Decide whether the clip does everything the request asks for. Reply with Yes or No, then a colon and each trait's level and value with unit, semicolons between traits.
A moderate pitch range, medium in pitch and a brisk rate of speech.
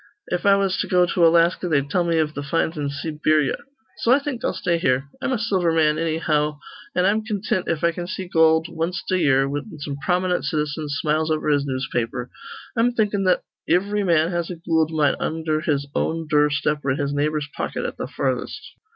Yes: average, 3.3 semitones; medium, 160 Hz; fast, 210 wpm